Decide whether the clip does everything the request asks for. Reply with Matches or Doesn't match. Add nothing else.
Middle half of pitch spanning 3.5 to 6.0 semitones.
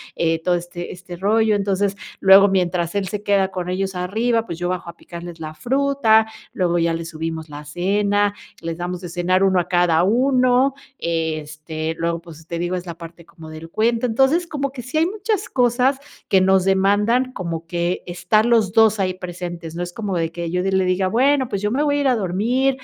Matches